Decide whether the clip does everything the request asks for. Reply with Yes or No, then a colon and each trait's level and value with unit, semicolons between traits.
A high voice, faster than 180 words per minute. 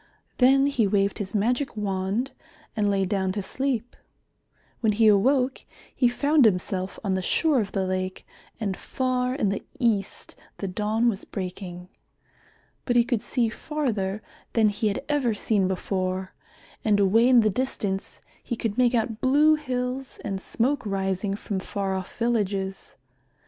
No: high, 215 Hz; average, 155 wpm